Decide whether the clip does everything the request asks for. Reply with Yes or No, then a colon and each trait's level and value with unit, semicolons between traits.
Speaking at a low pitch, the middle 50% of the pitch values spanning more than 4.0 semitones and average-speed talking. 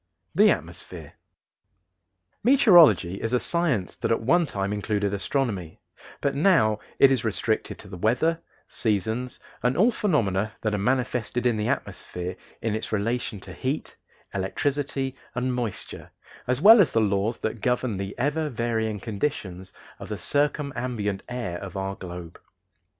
Yes: low, 115 Hz; average, 5.1 semitones; average, 145 wpm